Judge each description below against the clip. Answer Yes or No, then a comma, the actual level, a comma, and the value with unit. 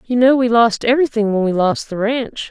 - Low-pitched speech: No, high, 230 Hz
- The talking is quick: Yes, fast, 240 wpm